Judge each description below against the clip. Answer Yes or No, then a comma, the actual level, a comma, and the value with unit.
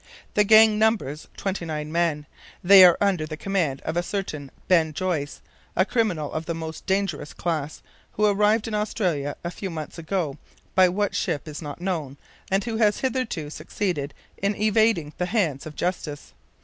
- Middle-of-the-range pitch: Yes, medium, 175 Hz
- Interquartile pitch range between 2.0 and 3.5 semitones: No, average, 4.8 semitones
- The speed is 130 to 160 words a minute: No, average, 175 wpm